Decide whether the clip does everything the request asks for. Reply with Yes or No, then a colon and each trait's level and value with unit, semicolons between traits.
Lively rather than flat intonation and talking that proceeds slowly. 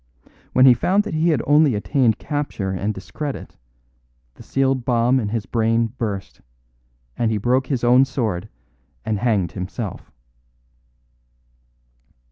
No: average, 4.2 semitones; slow, 130 wpm